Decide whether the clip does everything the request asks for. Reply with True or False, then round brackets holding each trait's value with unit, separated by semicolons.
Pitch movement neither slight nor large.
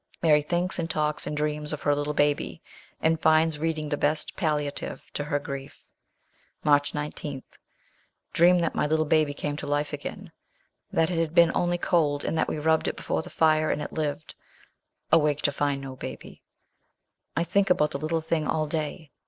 False (1.7 semitones)